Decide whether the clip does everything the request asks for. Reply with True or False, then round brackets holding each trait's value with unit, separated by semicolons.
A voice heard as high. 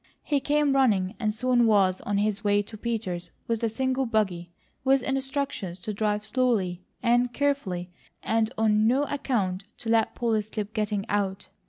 True (220 Hz)